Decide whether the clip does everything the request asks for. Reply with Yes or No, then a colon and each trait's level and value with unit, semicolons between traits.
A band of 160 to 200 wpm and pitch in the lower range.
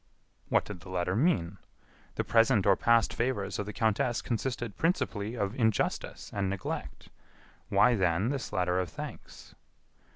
No: average, 150 wpm; low, 105 Hz